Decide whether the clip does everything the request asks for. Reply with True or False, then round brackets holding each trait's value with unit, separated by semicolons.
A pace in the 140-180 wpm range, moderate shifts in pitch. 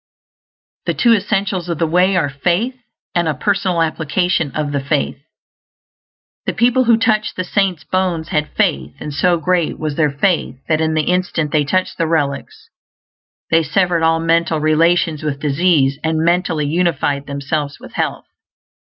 True (160 wpm; 3.3 semitones)